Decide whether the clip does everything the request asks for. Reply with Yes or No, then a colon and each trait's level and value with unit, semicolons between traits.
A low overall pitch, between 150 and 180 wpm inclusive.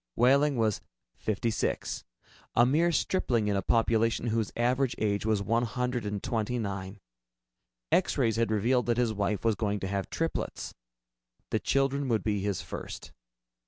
Yes: low, 115 Hz; average, 160 wpm